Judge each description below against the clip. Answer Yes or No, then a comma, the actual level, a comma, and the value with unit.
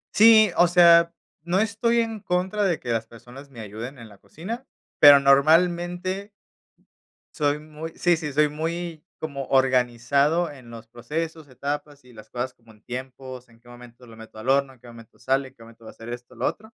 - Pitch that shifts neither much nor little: No, wide, 5.9 semitones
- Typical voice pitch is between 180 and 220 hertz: No, medium, 140 Hz